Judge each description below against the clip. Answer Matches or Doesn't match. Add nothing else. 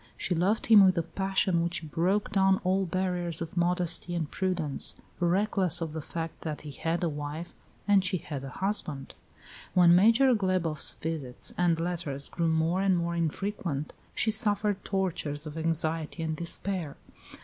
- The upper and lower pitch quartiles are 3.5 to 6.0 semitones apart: Doesn't match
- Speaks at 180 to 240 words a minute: Doesn't match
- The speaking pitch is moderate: Matches